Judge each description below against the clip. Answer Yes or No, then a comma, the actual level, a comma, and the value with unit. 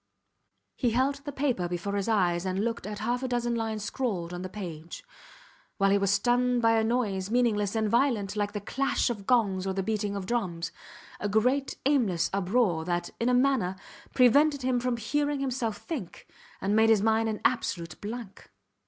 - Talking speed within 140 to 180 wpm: No, average, 190 wpm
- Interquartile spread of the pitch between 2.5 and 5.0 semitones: Yes, average, 4.1 semitones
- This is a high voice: Yes, high, 220 Hz